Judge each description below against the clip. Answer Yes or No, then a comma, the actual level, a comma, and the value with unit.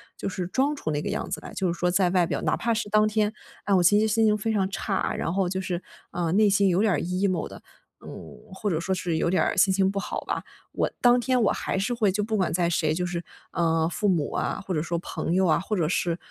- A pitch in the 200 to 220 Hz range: No, high, 190 Hz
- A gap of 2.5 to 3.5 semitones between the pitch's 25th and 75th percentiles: Yes, average, 3.2 semitones